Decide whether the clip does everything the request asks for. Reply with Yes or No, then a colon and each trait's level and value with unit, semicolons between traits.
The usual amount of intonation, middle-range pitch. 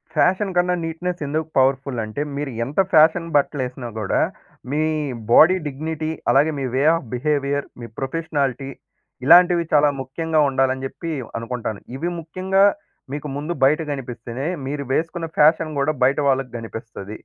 Yes: average, 3.6 semitones; medium, 145 Hz